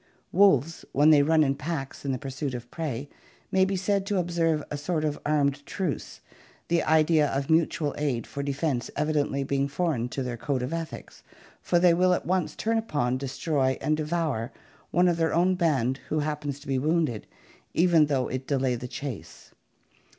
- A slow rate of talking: No, average, 185 wpm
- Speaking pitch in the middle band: Yes, medium, 150 Hz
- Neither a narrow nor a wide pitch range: Yes, average, 3.6 semitones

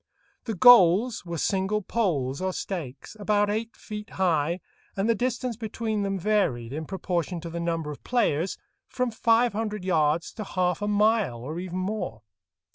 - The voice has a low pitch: No, high, 190 Hz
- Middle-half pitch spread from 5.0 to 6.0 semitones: No, average, 4.4 semitones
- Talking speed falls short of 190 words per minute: Yes, average, 165 wpm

